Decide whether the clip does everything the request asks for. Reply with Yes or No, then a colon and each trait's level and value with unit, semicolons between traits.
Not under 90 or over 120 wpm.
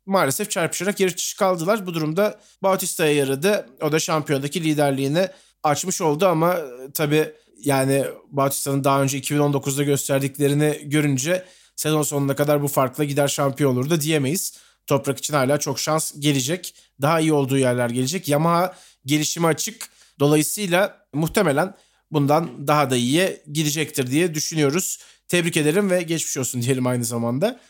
No: fast, 140 wpm